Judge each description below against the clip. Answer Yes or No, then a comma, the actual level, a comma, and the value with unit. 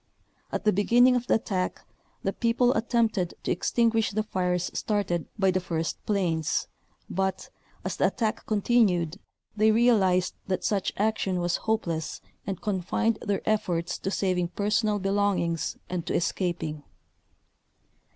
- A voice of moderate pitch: No, high, 195 Hz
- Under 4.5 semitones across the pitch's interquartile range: Yes, average, 3.4 semitones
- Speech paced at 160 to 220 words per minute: No, average, 140 wpm